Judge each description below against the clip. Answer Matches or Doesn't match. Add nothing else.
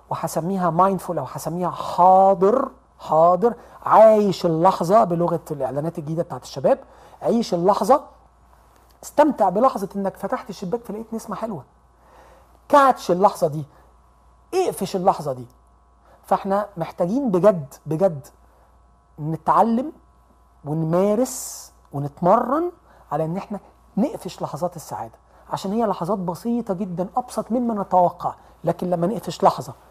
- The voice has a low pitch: Doesn't match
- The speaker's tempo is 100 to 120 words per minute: Matches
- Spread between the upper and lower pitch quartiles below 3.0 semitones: Doesn't match